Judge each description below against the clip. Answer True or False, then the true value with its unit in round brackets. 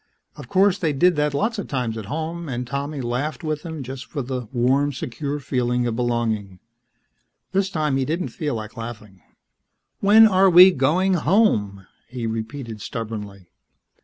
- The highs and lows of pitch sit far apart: True (5.7 semitones)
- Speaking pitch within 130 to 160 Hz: True (135 Hz)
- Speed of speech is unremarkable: True (160 wpm)